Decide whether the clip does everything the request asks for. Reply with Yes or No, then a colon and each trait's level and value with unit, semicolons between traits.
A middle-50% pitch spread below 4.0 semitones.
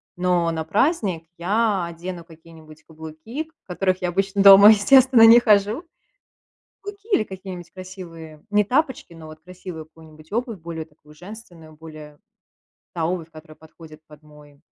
No: average, 4.3 semitones